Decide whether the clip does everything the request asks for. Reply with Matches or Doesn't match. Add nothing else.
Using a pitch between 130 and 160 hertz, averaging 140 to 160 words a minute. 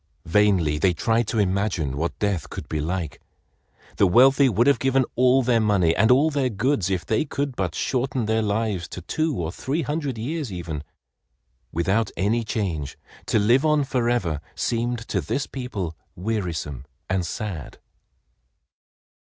Doesn't match